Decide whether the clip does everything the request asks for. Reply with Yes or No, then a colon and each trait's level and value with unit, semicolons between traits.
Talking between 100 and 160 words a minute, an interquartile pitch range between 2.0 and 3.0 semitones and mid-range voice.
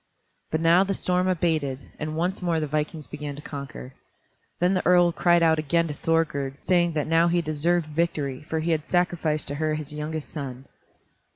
No: average, 185 wpm; narrow, 2.5 semitones; medium, 160 Hz